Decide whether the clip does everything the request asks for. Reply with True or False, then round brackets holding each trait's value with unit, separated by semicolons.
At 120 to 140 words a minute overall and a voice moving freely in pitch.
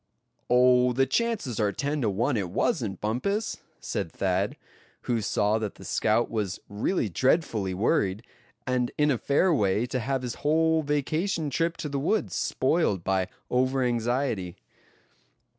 False (150 wpm; 5.8 semitones)